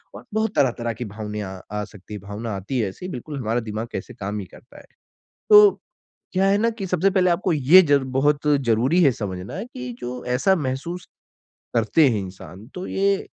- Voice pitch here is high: No, low, 125 Hz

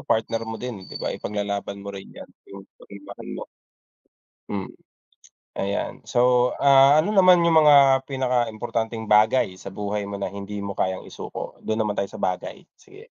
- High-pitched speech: No, low, 110 Hz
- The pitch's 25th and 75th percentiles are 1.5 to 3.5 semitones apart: No, average, 4.9 semitones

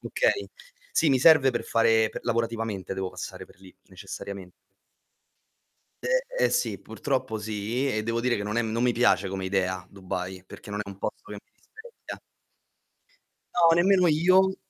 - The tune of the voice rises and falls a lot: Yes, wide, 7.9 semitones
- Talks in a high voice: No, low, 115 Hz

